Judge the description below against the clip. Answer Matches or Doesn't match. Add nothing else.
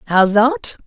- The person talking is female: Matches